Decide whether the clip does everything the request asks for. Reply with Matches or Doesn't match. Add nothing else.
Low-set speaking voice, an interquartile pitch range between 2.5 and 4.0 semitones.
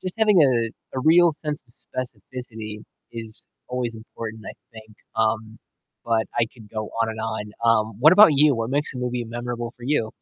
Matches